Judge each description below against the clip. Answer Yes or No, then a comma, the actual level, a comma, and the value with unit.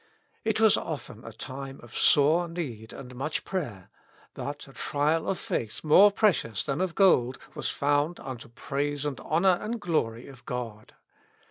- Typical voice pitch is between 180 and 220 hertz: No, medium, 145 Hz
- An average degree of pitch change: No, wide, 5.8 semitones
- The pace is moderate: Yes, average, 160 wpm